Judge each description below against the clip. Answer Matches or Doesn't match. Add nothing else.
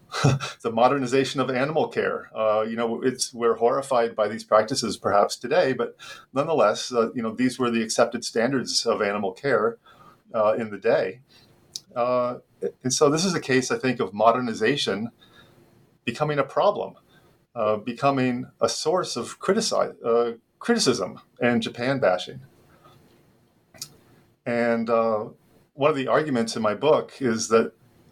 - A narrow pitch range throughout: Matches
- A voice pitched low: Matches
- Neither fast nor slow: Matches